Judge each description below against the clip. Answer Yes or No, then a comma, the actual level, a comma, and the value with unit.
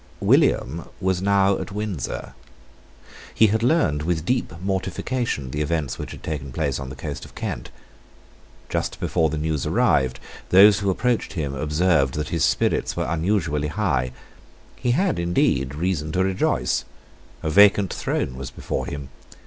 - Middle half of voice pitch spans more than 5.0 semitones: Yes, wide, 5.4 semitones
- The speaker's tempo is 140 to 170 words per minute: Yes, average, 155 wpm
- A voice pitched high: No, very low, 80 Hz